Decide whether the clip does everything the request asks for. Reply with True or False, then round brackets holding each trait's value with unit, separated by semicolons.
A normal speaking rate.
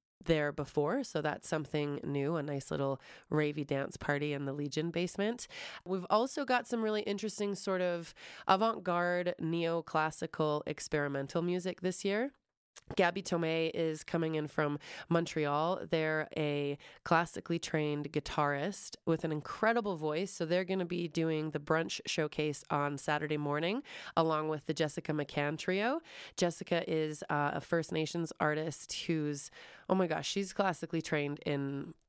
True (150 wpm)